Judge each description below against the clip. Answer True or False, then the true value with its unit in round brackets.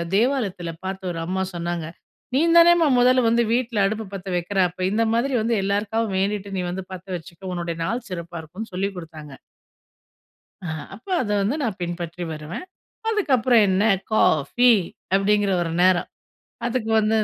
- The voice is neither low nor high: False (195 Hz)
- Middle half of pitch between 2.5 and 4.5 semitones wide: False (4.9 semitones)